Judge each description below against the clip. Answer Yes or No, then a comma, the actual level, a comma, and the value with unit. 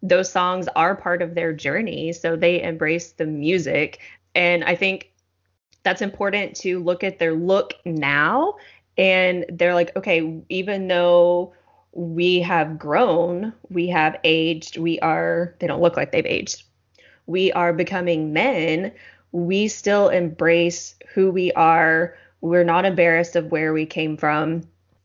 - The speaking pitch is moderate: Yes, medium, 175 Hz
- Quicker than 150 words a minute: No, average, 145 wpm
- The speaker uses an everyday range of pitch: No, narrow, 1.9 semitones